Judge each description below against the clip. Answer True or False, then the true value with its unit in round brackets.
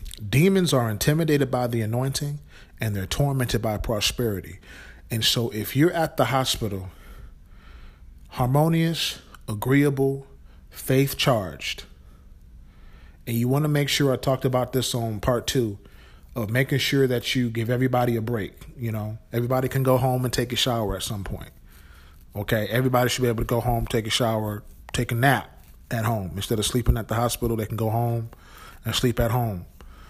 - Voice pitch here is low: True (115 Hz)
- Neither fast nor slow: True (175 wpm)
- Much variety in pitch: False (4.8 semitones)